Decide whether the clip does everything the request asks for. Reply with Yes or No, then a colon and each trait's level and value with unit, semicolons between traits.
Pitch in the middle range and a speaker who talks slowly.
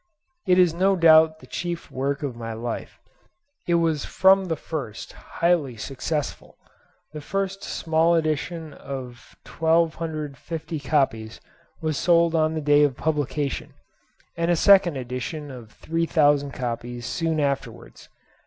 Yes: medium, 155 Hz; slow, 130 wpm